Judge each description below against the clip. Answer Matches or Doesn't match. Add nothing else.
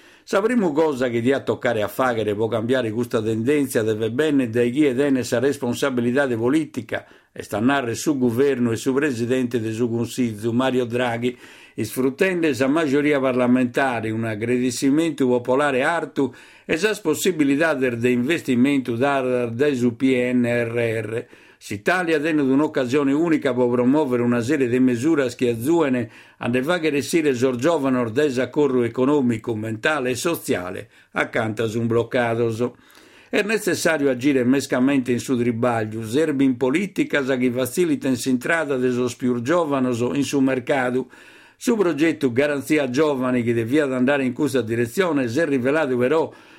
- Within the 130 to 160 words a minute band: Matches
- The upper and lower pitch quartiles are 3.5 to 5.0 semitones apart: Doesn't match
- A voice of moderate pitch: Doesn't match